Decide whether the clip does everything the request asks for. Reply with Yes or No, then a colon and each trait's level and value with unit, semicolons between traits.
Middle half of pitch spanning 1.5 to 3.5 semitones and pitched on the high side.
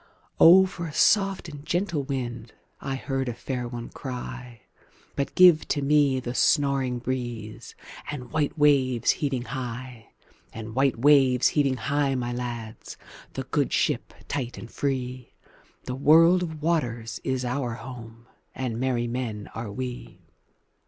No: average, 3.1 semitones; low, 130 Hz